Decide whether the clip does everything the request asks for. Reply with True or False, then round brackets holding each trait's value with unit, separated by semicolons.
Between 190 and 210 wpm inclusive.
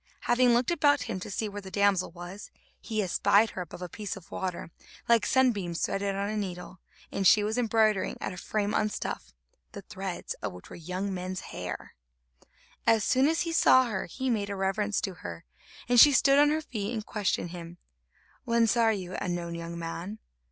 True (200 wpm)